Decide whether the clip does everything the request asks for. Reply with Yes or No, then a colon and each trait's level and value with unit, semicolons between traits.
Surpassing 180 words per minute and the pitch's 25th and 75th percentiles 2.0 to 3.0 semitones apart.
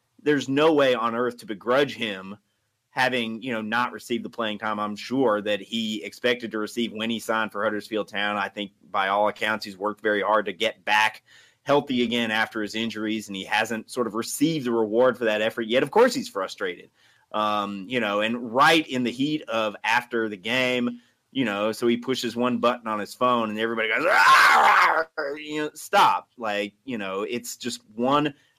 Yes: fast, 205 wpm; narrow, 2.5 semitones